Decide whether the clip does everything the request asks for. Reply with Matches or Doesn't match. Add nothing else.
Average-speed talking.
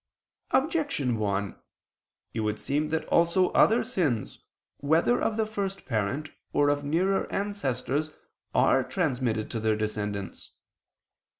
Doesn't match